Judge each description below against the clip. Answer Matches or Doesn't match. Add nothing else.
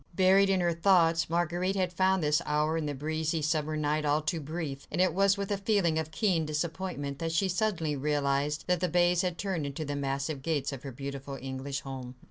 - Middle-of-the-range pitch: Matches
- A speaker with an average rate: Doesn't match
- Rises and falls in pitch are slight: Doesn't match